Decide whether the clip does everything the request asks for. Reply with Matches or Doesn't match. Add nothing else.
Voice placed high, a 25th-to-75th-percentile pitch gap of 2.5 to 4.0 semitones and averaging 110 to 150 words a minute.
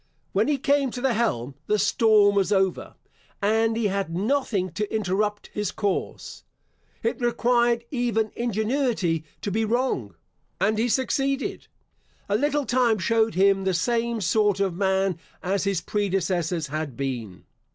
Matches